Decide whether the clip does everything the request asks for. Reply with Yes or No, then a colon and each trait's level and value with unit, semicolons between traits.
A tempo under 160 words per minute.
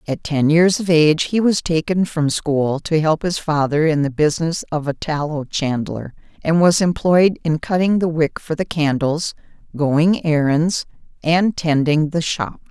No: average, 175 wpm